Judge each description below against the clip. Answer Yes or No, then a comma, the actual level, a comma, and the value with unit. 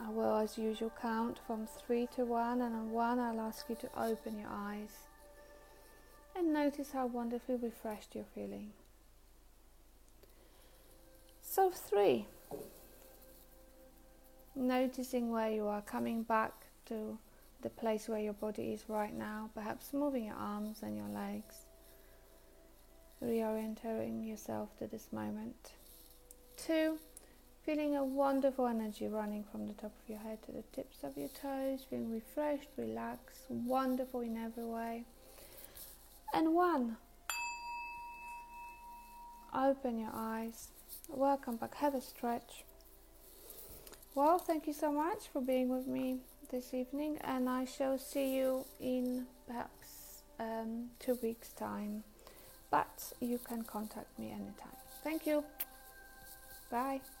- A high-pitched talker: Yes, high, 245 Hz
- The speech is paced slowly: Yes, slow, 125 wpm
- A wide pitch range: No, average, 3.9 semitones